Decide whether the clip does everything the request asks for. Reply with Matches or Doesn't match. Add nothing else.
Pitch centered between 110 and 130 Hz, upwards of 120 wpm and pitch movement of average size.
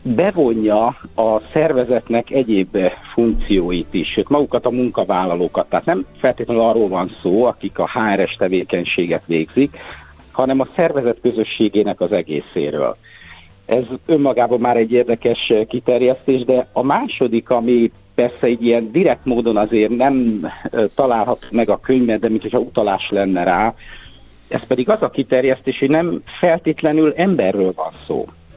Matches